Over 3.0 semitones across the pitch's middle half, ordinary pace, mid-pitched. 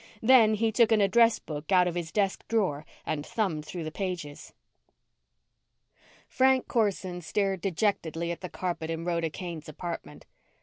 Yes: average, 4.5 semitones; average, 155 wpm; medium, 180 Hz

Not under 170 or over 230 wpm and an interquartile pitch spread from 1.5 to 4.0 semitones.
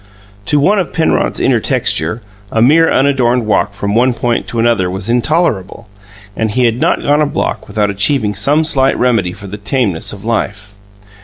No: average, 180 wpm; average, 4.7 semitones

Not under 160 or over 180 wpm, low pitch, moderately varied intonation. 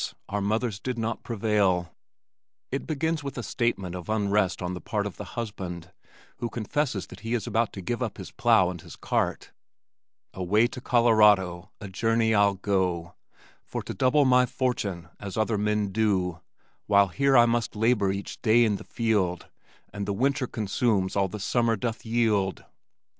Yes: average, 175 wpm; low, 105 Hz; average, 3.5 semitones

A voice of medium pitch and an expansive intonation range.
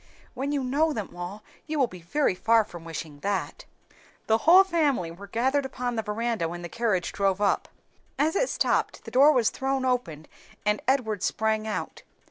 No: high, 225 Hz; wide, 5.7 semitones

